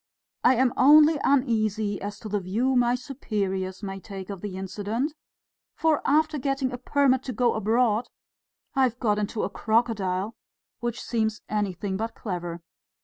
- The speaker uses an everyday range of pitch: Yes, average, 4.2 semitones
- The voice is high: Yes, high, 220 Hz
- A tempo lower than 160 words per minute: Yes, average, 150 wpm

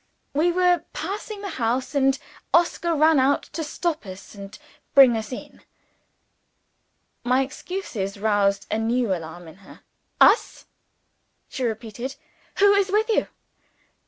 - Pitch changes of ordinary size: No, wide, 8.1 semitones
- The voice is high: Yes, very high, 265 Hz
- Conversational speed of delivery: No, slow, 130 wpm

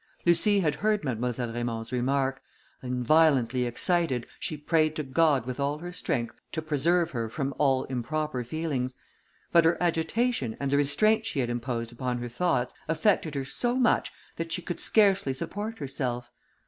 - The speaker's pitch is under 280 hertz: Yes, medium, 140 Hz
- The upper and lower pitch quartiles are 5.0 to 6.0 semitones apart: Yes, average, 5.3 semitones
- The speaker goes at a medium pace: Yes, average, 165 wpm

